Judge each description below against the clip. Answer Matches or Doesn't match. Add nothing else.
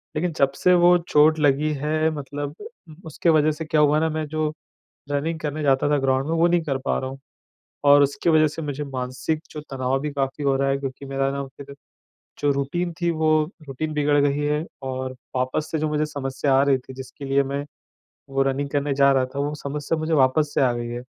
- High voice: Doesn't match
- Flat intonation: Matches